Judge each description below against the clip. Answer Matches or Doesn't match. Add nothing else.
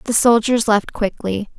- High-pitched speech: Matches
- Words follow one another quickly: Doesn't match